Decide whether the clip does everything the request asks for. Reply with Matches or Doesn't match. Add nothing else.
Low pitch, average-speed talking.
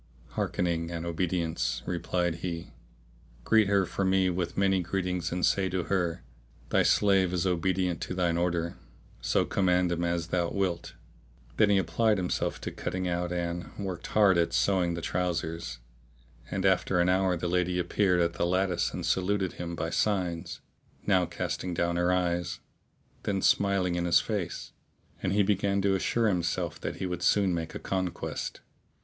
Matches